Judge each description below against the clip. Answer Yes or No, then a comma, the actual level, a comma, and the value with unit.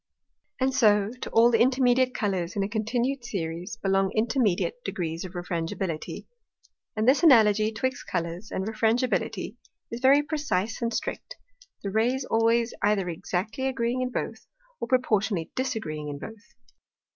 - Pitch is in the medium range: No, high, 220 Hz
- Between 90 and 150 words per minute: Yes, average, 145 wpm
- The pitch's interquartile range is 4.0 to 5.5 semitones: Yes, average, 4.7 semitones